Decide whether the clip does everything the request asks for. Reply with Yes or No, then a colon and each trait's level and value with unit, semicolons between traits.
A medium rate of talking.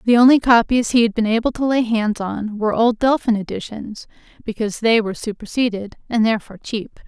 Yes: average, 185 wpm